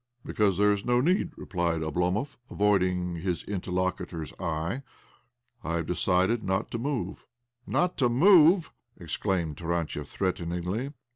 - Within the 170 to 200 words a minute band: No, average, 145 wpm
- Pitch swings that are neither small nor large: No, wide, 5.7 semitones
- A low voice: Yes, very low, 95 Hz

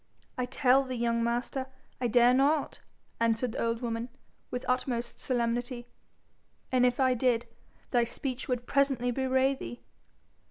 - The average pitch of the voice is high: Yes, high, 245 Hz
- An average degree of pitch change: No, narrow, 1.7 semitones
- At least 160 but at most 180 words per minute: No, average, 145 wpm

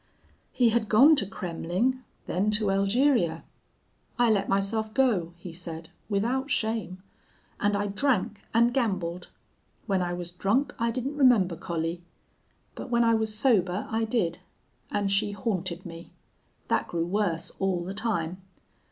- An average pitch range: Yes, average, 4.5 semitones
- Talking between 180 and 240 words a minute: No, average, 145 wpm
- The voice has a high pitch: Yes, high, 200 Hz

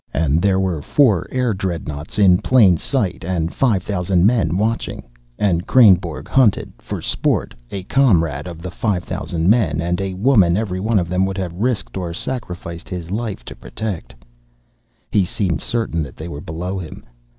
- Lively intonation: No, average, 3.9 semitones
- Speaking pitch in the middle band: No, very low, 95 Hz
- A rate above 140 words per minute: Yes, average, 175 wpm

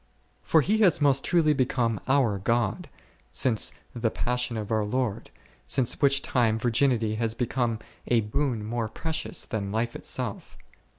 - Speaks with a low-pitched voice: Yes, low, 120 Hz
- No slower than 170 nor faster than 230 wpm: No, average, 155 wpm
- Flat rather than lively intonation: No, average, 3.5 semitones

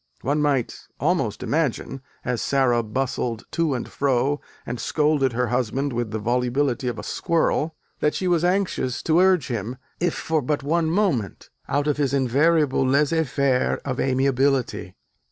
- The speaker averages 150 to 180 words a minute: Yes, average, 155 wpm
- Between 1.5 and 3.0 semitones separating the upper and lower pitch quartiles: No, average, 3.6 semitones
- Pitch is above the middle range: No, low, 135 Hz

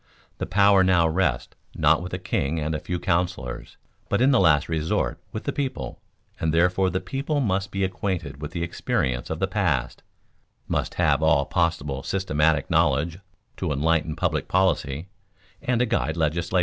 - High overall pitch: No, very low, 85 Hz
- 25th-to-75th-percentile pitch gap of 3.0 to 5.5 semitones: Yes, average, 3.7 semitones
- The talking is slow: No, average, 170 wpm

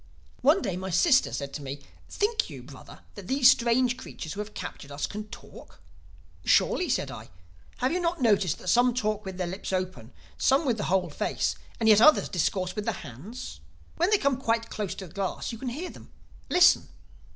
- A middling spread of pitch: No, wide, 5.9 semitones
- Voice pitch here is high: Yes, high, 215 Hz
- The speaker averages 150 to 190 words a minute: No, fast, 205 wpm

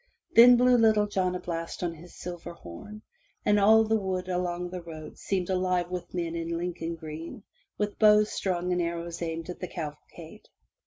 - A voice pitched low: No, medium, 180 Hz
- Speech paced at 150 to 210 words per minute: Yes, average, 180 wpm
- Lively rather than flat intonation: No, average, 3.3 semitones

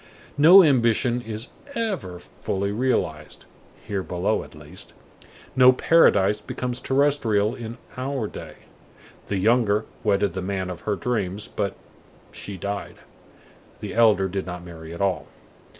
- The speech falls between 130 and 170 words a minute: Yes, slow, 135 wpm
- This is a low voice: Yes, low, 105 Hz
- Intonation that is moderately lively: Yes, average, 4.6 semitones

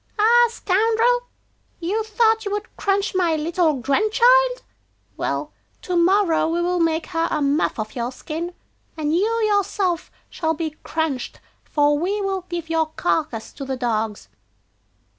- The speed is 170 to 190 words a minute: No, average, 145 wpm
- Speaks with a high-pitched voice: Yes, very high, 345 Hz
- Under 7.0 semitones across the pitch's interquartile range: Yes, average, 5.1 semitones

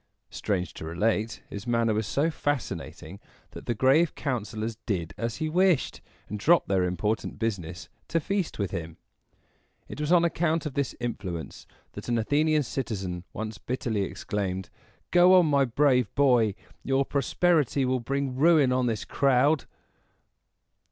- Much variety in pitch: Yes, wide, 5.9 semitones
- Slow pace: No, average, 150 wpm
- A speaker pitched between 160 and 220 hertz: No, low, 125 Hz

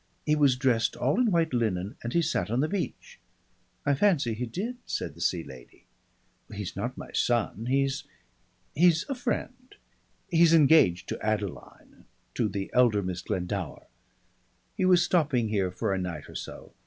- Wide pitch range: Yes, wide, 8.6 semitones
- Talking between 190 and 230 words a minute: No, average, 165 wpm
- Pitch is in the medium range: No, low, 125 Hz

